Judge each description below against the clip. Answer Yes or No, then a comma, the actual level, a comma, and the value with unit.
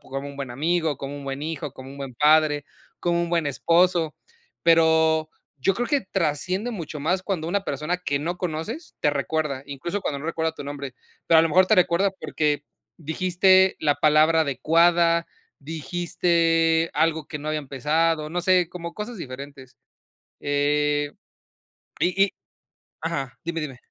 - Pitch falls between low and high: Yes, medium, 160 Hz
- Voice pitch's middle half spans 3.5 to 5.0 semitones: No, average, 3.0 semitones